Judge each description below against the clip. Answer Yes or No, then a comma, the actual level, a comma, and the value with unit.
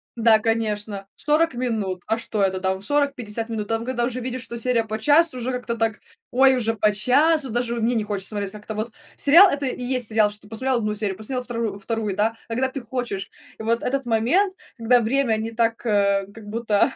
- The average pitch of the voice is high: Yes, high, 230 Hz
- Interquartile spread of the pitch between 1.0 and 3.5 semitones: Yes, average, 2.9 semitones